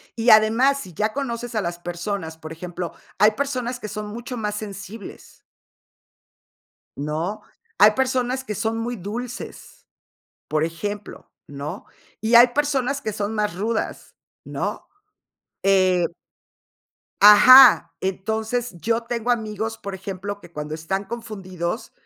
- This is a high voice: Yes, high, 215 Hz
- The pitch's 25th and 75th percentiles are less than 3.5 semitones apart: No, average, 4.1 semitones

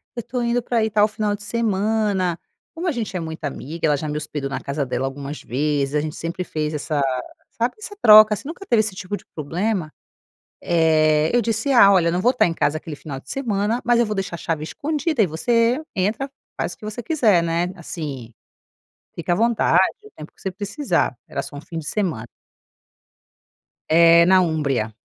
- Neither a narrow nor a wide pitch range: No, wide, 6.5 semitones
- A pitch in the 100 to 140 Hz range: No, medium, 185 Hz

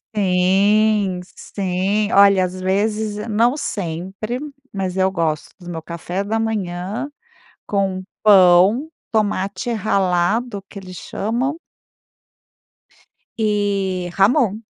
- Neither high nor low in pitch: No, high, 200 Hz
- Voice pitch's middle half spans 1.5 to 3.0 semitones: Yes, average, 2.7 semitones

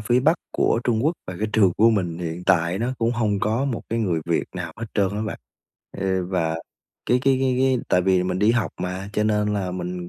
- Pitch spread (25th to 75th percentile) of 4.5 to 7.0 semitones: No, average, 4.1 semitones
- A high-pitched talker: No, low, 105 Hz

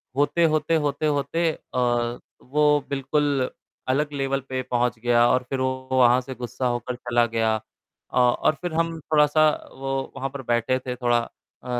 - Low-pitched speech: Yes, low, 130 Hz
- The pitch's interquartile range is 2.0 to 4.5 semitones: Yes, average, 3.2 semitones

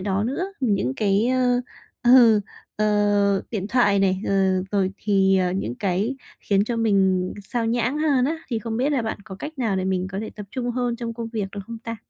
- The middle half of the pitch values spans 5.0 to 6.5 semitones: No, average, 3.7 semitones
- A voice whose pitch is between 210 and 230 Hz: Yes, high, 215 Hz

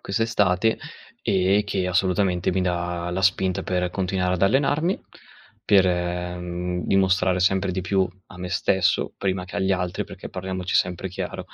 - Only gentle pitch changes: Yes, narrow, 1.3 semitones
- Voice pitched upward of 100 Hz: No, very low, 95 Hz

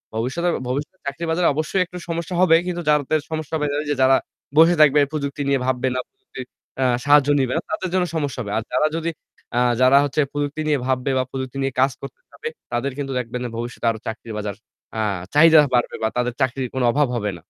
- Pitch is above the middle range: No, medium, 140 Hz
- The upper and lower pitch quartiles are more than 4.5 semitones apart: No, average, 3.6 semitones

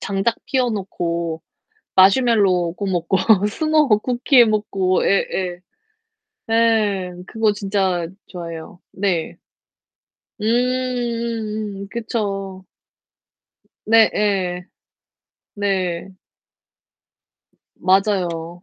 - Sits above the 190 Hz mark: Yes, high, 200 Hz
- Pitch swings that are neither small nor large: Yes, average, 3.7 semitones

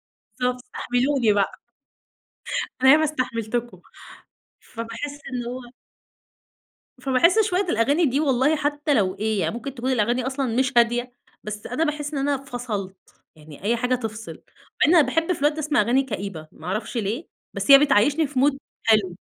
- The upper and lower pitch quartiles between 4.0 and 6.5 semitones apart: Yes, average, 4.3 semitones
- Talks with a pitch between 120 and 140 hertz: No, very high, 250 Hz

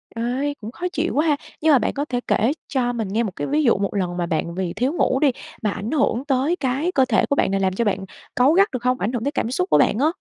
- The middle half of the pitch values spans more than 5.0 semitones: Yes, wide, 5.4 semitones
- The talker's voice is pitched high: Yes, very high, 250 Hz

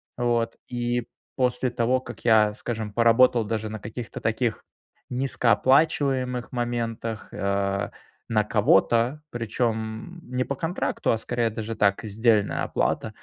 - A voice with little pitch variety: Yes, narrow, 2.2 semitones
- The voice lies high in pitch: No, low, 115 Hz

